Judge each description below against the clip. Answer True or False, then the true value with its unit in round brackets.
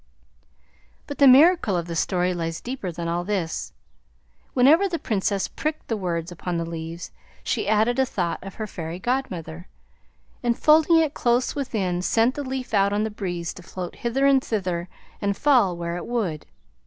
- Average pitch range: False (6.7 semitones)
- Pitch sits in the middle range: False (200 Hz)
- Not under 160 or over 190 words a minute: True (180 wpm)